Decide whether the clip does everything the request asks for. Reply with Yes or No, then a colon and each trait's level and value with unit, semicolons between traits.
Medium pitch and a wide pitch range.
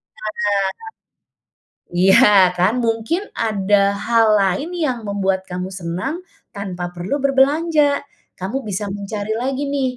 No: high, 215 Hz; wide, 5.9 semitones